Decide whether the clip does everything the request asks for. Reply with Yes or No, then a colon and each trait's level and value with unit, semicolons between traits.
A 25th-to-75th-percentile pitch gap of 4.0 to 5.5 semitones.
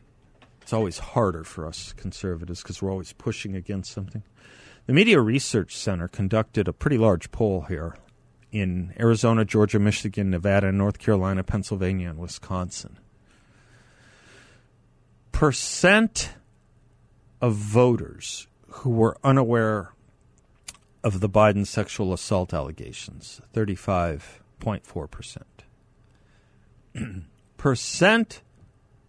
No: average, 3.4 semitones